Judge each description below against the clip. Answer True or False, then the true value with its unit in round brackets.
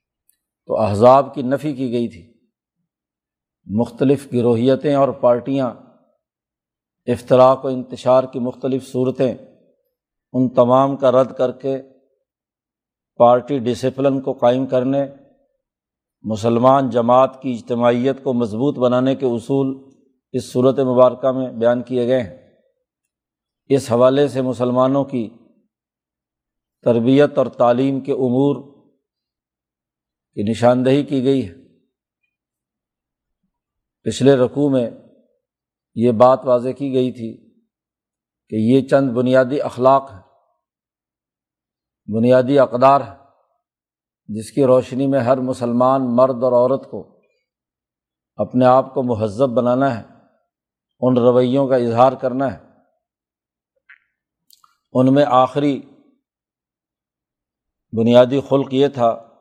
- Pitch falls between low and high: False (130 Hz)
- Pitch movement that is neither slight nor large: False (1.9 semitones)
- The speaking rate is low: True (105 wpm)